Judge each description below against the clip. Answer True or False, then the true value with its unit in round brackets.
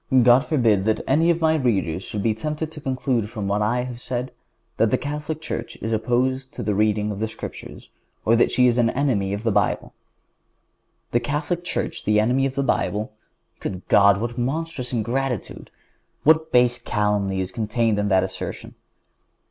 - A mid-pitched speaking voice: False (120 Hz)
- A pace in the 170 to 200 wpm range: True (180 wpm)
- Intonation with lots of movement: False (4.2 semitones)